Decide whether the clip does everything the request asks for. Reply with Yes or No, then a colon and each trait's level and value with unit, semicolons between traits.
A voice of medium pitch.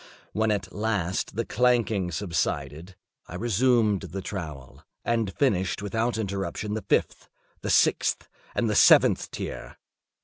No: low, 105 Hz